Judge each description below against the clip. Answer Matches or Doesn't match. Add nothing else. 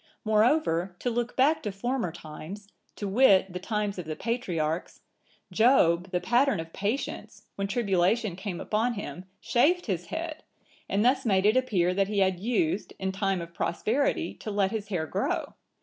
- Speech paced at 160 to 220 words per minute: Matches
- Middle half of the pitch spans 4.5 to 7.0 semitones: Matches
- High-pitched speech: Matches